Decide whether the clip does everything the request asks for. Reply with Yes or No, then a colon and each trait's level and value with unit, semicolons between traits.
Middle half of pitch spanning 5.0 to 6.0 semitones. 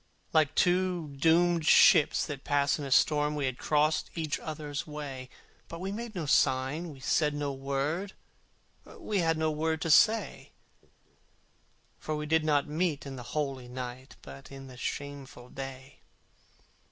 No: average, 2.9 semitones